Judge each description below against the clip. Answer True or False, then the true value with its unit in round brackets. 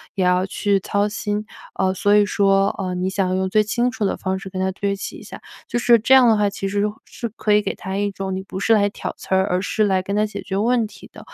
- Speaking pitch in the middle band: False (200 Hz)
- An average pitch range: False (1.8 semitones)